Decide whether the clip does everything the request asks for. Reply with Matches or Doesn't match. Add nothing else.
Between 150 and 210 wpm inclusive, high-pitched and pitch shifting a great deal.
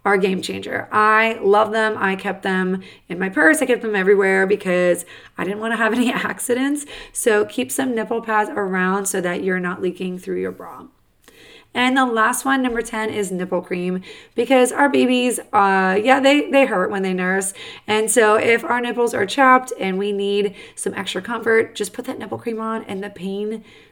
Doesn't match